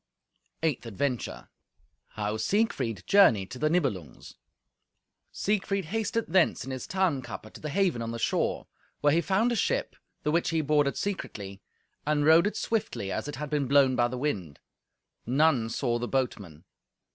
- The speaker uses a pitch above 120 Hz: Yes, medium, 140 Hz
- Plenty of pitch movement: Yes, wide, 6.7 semitones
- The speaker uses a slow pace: No, average, 160 wpm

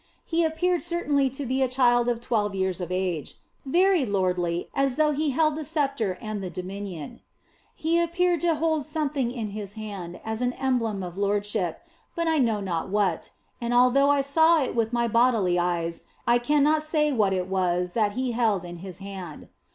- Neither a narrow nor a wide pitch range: No, wide, 7.2 semitones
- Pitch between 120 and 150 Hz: No, high, 235 Hz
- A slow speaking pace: No, average, 190 wpm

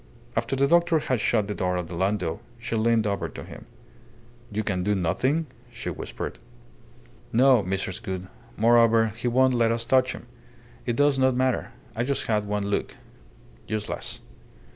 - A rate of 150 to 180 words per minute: Yes, average, 165 wpm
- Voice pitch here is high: No, low, 115 Hz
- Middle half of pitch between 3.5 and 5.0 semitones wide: Yes, average, 4.2 semitones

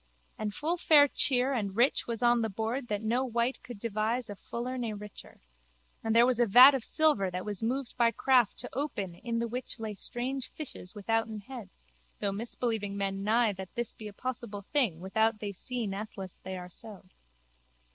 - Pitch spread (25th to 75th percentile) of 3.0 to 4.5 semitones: Yes, average, 3.4 semitones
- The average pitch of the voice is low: No, high, 225 Hz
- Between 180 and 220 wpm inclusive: Yes, average, 195 wpm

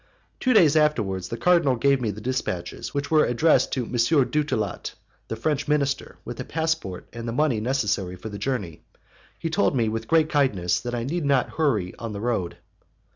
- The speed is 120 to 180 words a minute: No, average, 190 wpm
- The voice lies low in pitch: Yes, low, 125 Hz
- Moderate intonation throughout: No, wide, 5.8 semitones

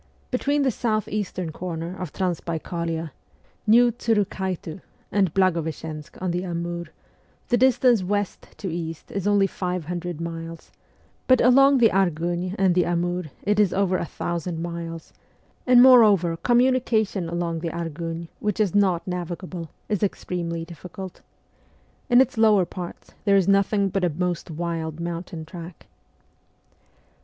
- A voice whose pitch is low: No, medium, 180 Hz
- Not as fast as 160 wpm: Yes, average, 140 wpm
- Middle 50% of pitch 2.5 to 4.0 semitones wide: Yes, average, 3.4 semitones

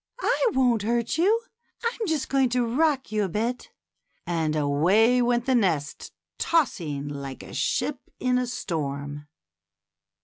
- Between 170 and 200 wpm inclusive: No, average, 140 wpm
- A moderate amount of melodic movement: No, wide, 9.0 semitones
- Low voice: No, high, 235 Hz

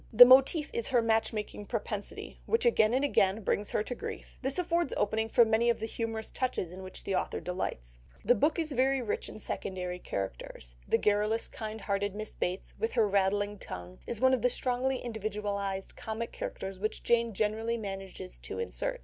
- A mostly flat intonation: No, average, 3.9 semitones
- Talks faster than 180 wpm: Yes, average, 190 wpm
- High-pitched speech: Yes, high, 220 Hz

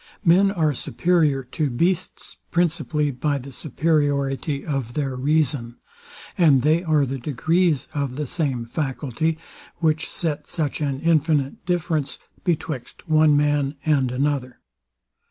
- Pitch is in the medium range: Yes, medium, 150 Hz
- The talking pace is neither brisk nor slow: No, slow, 125 wpm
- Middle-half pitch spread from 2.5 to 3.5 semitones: Yes, average, 2.9 semitones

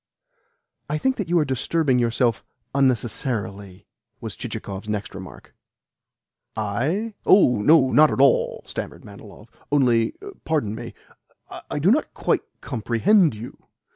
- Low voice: Yes, low, 125 Hz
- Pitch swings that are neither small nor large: No, wide, 6.1 semitones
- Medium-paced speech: No, slow, 125 wpm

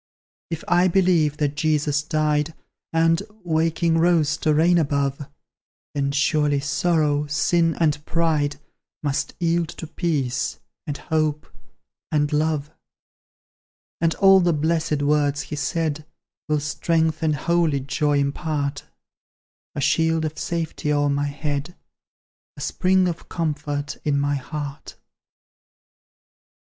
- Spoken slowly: Yes, slow, 120 wpm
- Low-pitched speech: No, medium, 155 Hz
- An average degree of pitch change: No, narrow, 2.2 semitones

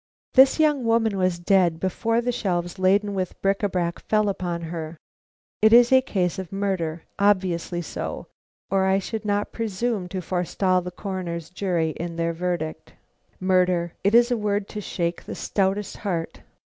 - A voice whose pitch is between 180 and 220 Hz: Yes, high, 190 Hz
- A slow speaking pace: No, average, 170 wpm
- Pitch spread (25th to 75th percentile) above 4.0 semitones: No, average, 3.0 semitones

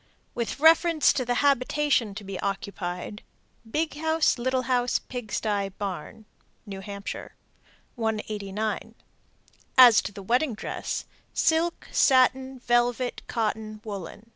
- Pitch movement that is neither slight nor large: Yes, average, 4.1 semitones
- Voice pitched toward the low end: No, high, 230 Hz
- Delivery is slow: Yes, slow, 115 wpm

